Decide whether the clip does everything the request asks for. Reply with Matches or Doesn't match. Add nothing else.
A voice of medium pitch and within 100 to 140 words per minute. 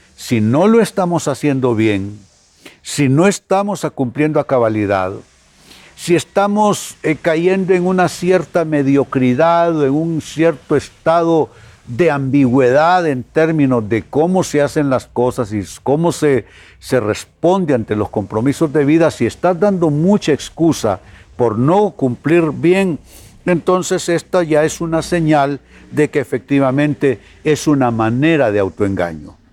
Matches